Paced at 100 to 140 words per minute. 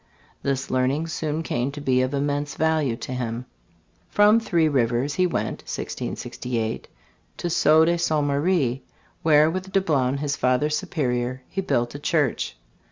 No: average, 150 wpm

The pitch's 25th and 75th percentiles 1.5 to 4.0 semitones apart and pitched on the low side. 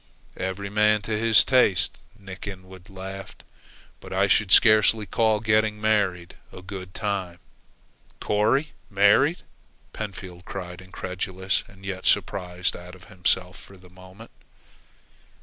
Yes: narrow, 2.5 semitones; very low, 95 Hz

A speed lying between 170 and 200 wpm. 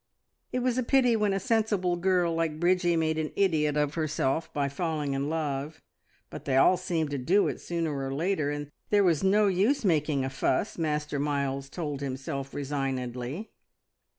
Yes: average, 180 wpm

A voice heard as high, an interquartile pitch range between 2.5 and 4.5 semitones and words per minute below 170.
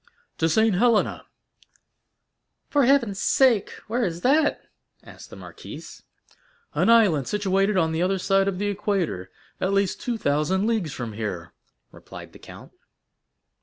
No: high, 195 Hz; average, 5.3 semitones; average, 140 wpm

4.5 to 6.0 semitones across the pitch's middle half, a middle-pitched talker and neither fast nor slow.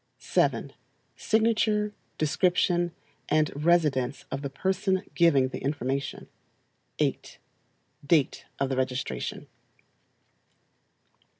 No: average, 5.2 semitones; medium, 155 Hz; slow, 85 wpm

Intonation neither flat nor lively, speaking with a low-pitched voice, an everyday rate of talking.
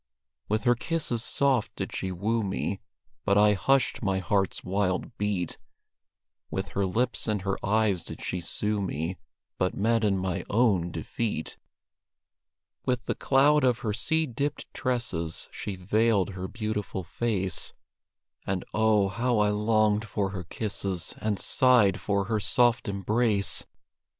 Yes: average, 3.3 semitones; low, 105 Hz; average, 145 wpm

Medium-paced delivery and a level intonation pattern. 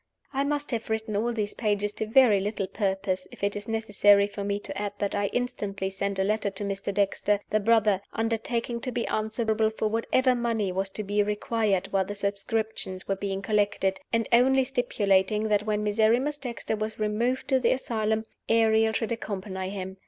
Yes: average, 190 wpm; narrow, 2.2 semitones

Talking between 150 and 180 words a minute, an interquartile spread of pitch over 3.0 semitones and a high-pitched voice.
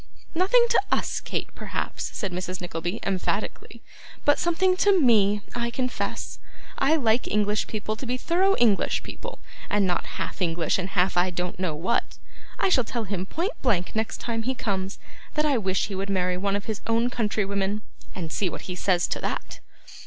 No: average, 190 wpm; average, 4.8 semitones; high, 210 Hz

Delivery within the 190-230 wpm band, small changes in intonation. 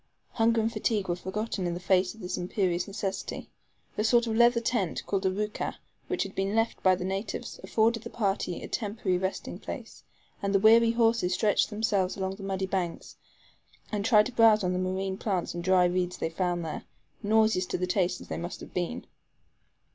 No: average, 200 wpm; average, 3.2 semitones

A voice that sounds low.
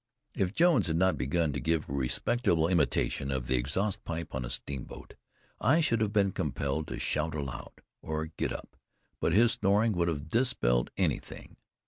Yes: very low, 80 Hz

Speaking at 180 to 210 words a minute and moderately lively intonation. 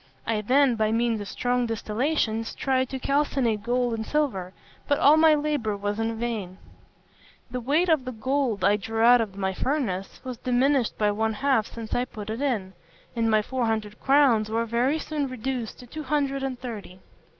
Yes: average, 190 wpm; average, 3.8 semitones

